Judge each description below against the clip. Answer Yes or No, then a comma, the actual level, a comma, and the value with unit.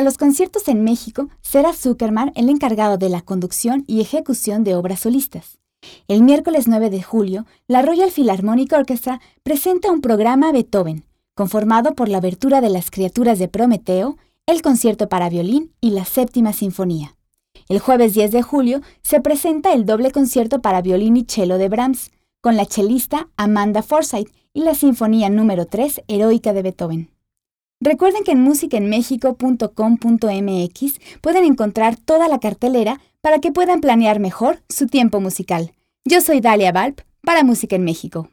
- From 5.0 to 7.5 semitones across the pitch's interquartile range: Yes, wide, 5.5 semitones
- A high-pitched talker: Yes, high, 235 Hz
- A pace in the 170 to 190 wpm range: No, average, 155 wpm